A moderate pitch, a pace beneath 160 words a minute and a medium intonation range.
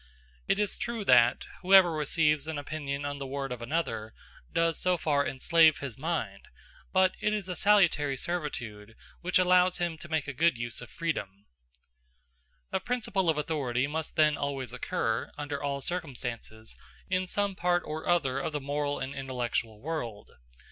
No: medium, 150 Hz; average, 165 wpm; average, 4.8 semitones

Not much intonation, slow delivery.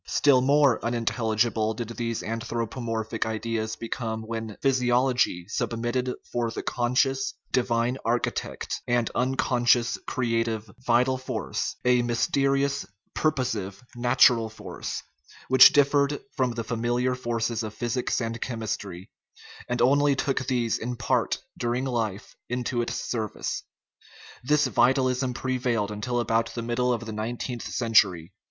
Yes: narrow, 2.1 semitones; slow, 125 wpm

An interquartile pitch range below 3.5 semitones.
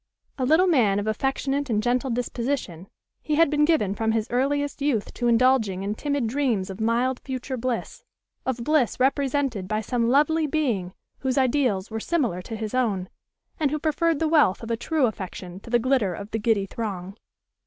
No: average, 4.9 semitones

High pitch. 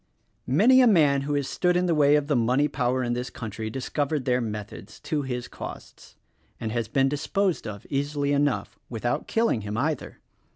No: low, 135 Hz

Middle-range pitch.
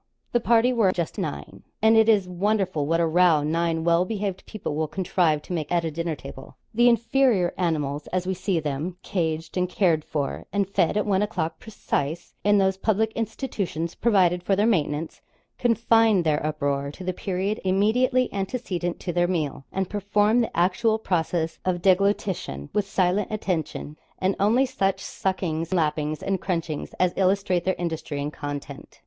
Yes: medium, 180 Hz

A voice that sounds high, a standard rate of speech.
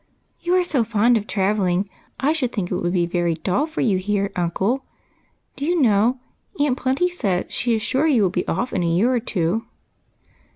No: high, 215 Hz; fast, 210 wpm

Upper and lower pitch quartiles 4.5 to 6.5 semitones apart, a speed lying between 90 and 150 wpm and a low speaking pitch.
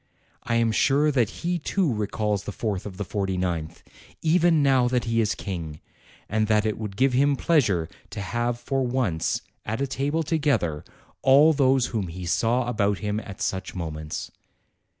No: wide, 5.6 semitones; average, 175 wpm; low, 115 Hz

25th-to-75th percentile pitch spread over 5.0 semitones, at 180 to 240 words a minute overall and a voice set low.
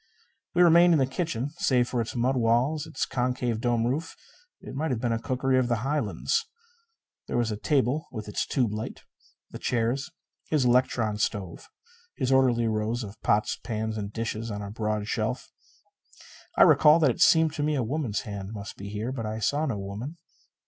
No: average, 4.0 semitones; average, 195 wpm; low, 120 Hz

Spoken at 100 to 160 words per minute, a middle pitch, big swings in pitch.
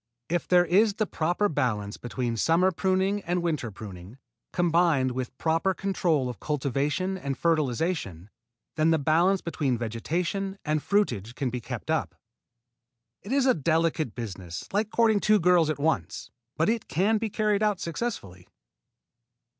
Yes: average, 150 wpm; medium, 165 Hz; wide, 6.9 semitones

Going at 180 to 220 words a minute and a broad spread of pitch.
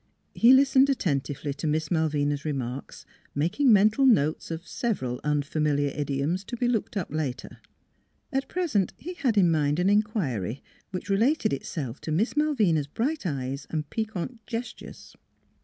No: average, 155 wpm; wide, 7.9 semitones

